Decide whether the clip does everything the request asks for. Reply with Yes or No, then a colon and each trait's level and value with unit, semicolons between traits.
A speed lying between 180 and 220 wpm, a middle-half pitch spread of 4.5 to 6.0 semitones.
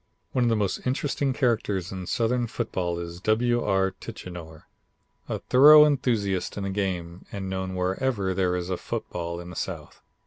No: average, 170 wpm; average, 4.9 semitones